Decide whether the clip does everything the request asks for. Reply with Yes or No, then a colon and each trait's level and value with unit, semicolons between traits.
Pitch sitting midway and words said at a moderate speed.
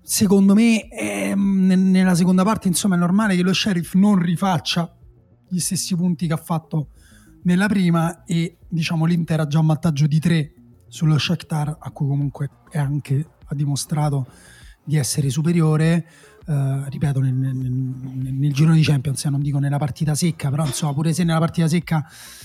No: medium, 160 Hz; fast, 175 wpm